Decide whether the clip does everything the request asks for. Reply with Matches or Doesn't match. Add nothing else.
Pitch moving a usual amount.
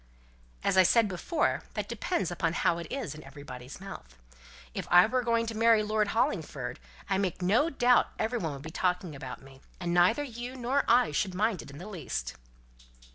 Doesn't match